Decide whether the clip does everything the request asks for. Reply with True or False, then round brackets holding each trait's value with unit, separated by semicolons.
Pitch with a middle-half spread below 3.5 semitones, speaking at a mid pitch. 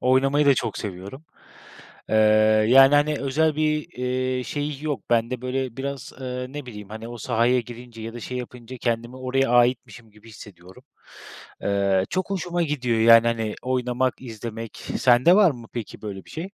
False (2.8 semitones; 125 Hz)